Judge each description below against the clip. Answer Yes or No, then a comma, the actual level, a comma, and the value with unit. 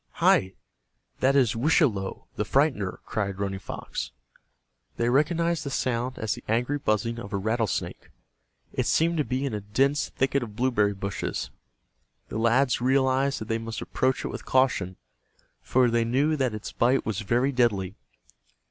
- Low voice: Yes, low, 120 Hz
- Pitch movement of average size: Yes, average, 3.9 semitones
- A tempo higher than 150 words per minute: Yes, average, 160 wpm